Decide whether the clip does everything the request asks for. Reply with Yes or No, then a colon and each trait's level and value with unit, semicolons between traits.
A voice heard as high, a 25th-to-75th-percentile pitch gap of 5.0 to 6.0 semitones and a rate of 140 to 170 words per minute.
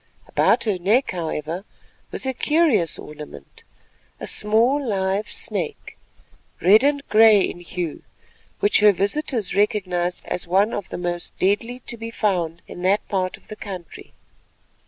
No: high, 200 Hz; average, 4.0 semitones; average, 145 wpm